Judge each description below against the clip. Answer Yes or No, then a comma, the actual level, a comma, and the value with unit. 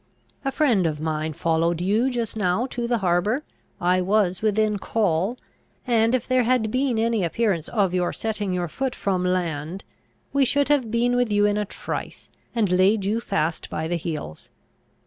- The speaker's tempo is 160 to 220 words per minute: Yes, average, 180 wpm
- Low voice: No, high, 205 Hz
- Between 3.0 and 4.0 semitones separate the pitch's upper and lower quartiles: No, average, 4.8 semitones